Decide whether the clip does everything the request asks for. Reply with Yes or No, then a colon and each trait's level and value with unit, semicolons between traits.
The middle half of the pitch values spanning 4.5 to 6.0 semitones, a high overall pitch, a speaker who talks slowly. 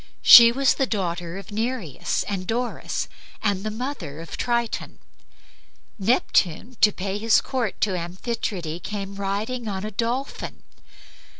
No: average, 4.1 semitones; high, 210 Hz; slow, 130 wpm